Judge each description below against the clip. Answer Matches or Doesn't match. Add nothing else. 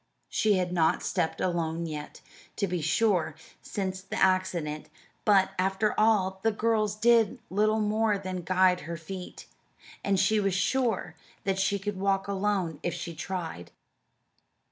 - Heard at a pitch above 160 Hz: Matches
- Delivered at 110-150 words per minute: Matches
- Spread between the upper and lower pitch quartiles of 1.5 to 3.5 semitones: Matches